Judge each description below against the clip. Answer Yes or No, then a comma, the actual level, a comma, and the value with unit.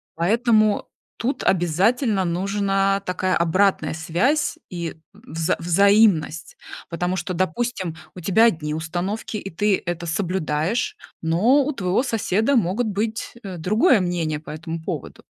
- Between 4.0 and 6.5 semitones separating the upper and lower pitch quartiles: Yes, average, 4.4 semitones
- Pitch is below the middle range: No, high, 190 Hz